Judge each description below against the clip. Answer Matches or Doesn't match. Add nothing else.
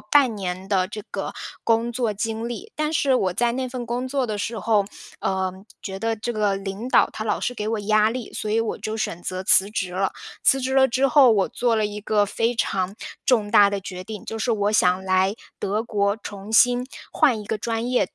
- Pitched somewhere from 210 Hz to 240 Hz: Matches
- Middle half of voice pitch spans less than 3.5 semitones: Matches